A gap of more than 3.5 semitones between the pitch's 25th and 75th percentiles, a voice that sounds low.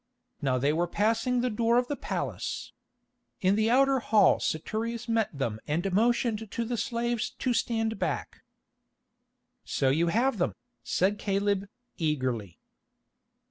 No: wide, 5.6 semitones; high, 215 Hz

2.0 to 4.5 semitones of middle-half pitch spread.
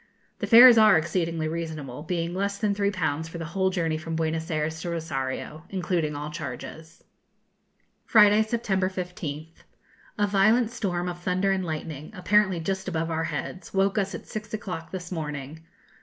Yes: average, 3.5 semitones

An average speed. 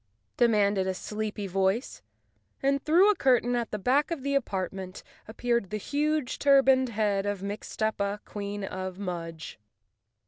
Yes: average, 145 wpm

